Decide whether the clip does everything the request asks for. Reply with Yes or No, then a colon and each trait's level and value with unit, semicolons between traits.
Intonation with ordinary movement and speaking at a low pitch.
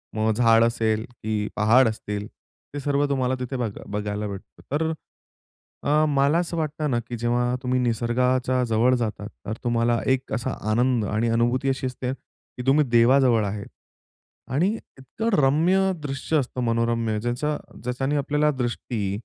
Yes: average, 3.1 semitones; low, 125 Hz